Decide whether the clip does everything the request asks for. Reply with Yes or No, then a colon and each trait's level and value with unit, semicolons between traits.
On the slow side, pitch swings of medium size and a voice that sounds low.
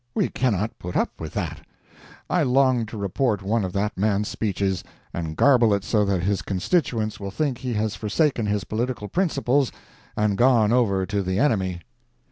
No: average, 175 wpm; average, 4.0 semitones; low, 105 Hz